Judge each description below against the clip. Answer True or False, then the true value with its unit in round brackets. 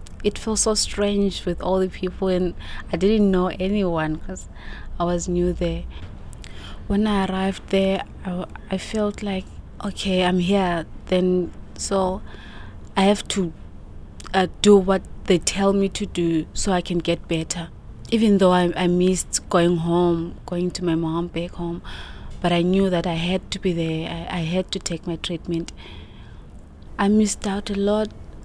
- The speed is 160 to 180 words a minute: True (170 wpm)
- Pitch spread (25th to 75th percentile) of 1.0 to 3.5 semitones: True (2.5 semitones)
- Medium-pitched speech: True (180 Hz)